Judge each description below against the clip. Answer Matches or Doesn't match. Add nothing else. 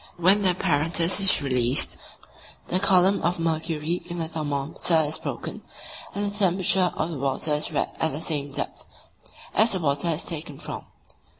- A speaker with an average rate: Matches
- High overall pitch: Doesn't match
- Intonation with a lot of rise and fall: Doesn't match